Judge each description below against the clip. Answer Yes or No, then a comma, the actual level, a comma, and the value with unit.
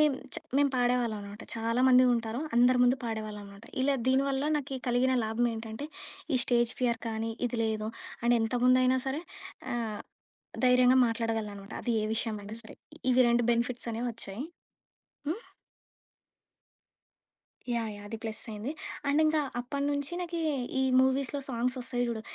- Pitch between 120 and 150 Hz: No, high, 240 Hz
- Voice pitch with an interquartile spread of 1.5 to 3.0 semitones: Yes, average, 2.7 semitones